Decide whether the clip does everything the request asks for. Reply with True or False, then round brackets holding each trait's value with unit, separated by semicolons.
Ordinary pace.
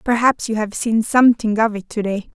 False (225 wpm)